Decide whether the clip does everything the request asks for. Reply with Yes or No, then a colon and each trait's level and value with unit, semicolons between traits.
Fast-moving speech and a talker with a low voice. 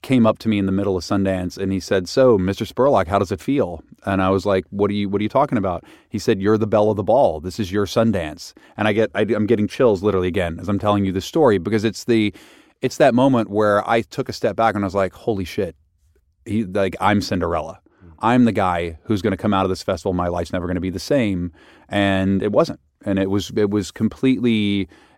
Yes: fast, 255 wpm; low, 100 Hz